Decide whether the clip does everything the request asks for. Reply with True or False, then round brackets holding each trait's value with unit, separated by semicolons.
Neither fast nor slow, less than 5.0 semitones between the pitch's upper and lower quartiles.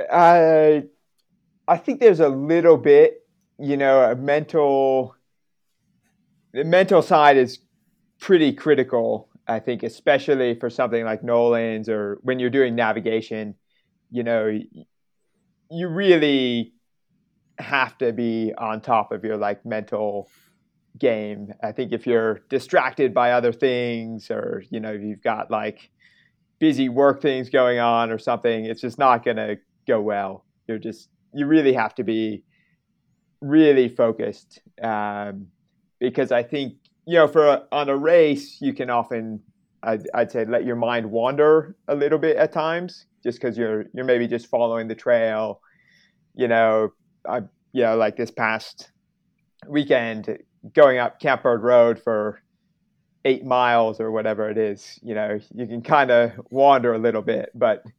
False (150 wpm; 5.6 semitones)